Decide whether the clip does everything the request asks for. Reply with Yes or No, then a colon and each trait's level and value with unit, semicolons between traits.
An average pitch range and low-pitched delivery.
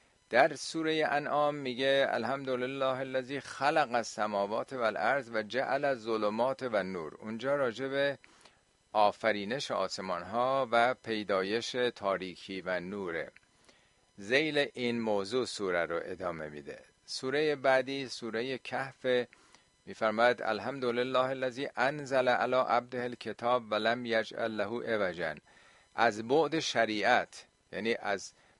Yes: average, 3.5 semitones; low, 125 Hz